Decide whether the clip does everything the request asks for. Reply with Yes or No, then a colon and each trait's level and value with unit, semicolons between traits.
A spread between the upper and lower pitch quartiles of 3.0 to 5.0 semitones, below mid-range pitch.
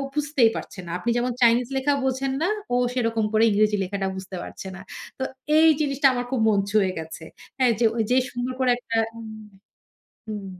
No: average, 3.7 semitones; high, 230 Hz